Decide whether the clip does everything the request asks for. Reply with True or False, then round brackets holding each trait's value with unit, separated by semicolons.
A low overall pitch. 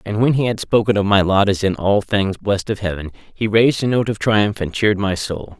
True (105 Hz)